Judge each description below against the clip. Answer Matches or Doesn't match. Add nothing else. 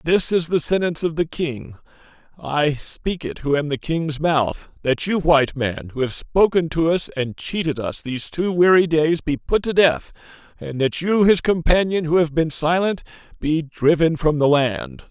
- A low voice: Doesn't match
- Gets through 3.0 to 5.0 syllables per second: Matches